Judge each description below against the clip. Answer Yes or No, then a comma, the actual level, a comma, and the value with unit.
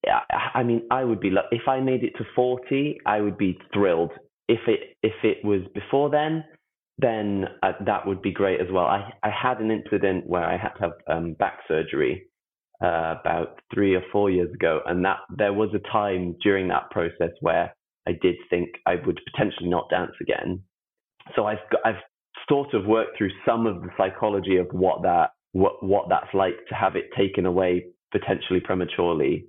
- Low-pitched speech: Yes, low, 100 Hz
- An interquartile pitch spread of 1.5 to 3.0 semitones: No, average, 4.0 semitones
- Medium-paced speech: Yes, average, 195 wpm